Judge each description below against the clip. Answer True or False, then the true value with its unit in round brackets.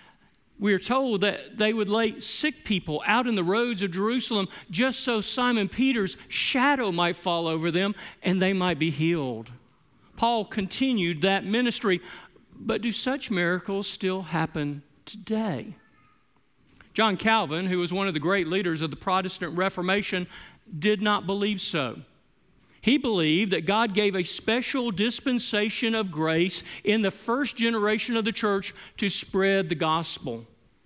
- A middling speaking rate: True (150 wpm)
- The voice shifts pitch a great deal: False (4.1 semitones)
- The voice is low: False (200 Hz)